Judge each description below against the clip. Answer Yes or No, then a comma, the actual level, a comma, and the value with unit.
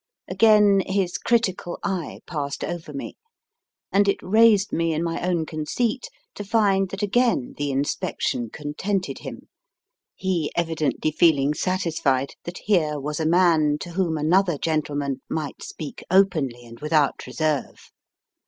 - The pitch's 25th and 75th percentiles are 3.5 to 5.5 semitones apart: Yes, average, 4.5 semitones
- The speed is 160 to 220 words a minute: No, slow, 135 wpm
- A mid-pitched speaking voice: Yes, medium, 165 Hz